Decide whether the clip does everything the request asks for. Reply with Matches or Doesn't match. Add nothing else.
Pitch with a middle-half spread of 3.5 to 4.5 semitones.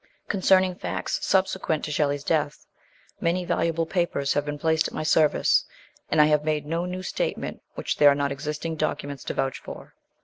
Doesn't match